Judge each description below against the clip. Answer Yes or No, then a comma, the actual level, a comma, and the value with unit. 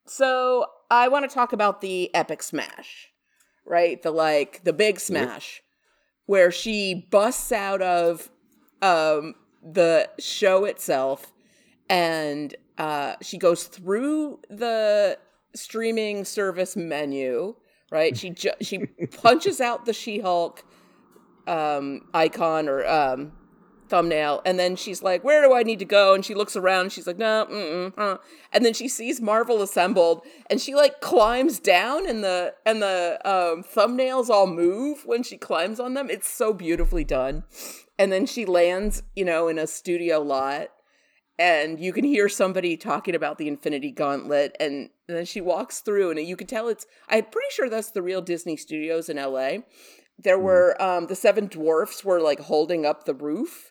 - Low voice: No, high, 190 Hz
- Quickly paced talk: No, average, 160 wpm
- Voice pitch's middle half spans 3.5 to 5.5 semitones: Yes, average, 5.2 semitones